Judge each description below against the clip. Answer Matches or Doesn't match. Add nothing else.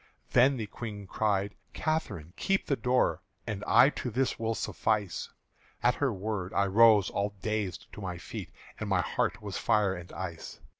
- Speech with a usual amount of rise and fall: Matches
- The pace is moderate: Matches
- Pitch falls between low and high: Doesn't match